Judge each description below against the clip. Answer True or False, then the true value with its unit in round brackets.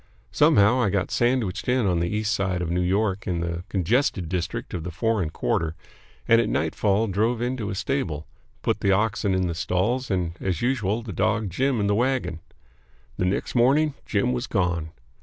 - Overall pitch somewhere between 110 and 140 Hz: False (100 Hz)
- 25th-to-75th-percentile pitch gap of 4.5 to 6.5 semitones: True (4.8 semitones)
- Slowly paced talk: False (190 wpm)